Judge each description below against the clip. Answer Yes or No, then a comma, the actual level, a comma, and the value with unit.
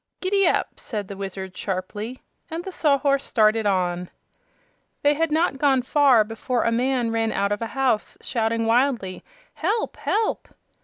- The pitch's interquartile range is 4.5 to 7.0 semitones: Yes, average, 5.2 semitones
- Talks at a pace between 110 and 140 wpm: No, average, 155 wpm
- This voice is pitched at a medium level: No, high, 235 Hz